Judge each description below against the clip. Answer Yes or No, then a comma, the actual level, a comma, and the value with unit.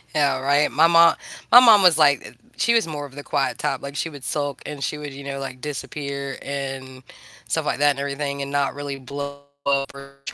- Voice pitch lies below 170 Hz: Yes, medium, 140 Hz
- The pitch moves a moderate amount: No, narrow, 1.3 semitones